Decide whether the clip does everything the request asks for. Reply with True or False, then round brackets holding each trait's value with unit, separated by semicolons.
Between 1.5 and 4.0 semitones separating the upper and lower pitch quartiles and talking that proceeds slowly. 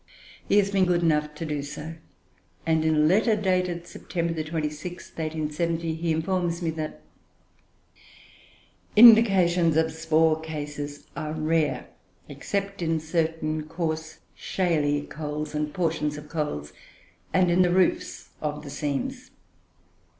True (2.5 semitones; 130 wpm)